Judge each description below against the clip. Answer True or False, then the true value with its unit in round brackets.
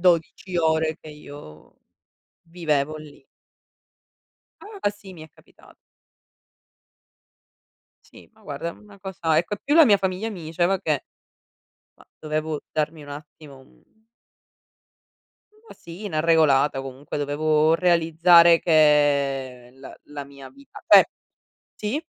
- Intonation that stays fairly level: False (3.4 semitones)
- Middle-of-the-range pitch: True (160 Hz)